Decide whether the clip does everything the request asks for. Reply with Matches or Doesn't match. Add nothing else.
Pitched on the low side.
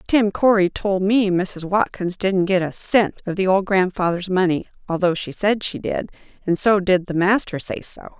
Doesn't match